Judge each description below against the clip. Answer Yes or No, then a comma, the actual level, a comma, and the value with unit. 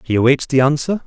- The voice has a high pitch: No, medium, 140 Hz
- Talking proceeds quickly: Yes, fast, 225 wpm